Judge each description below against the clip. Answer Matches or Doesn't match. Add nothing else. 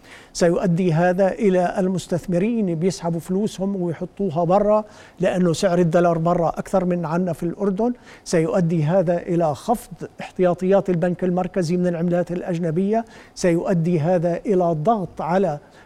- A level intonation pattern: Matches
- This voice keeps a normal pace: Matches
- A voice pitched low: Doesn't match